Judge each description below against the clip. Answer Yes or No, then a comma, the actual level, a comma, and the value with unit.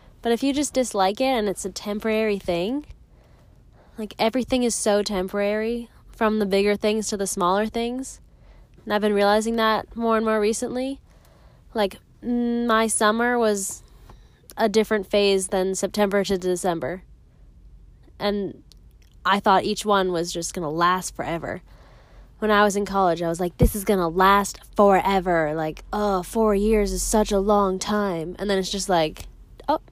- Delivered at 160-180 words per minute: Yes, average, 165 wpm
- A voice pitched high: Yes, high, 205 Hz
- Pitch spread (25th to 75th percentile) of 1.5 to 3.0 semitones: Yes, narrow, 2.6 semitones